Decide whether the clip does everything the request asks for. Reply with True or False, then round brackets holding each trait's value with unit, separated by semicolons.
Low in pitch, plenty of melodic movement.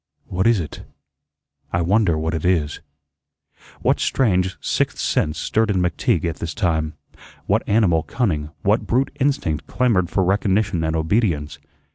False (90 Hz; 4.9 semitones)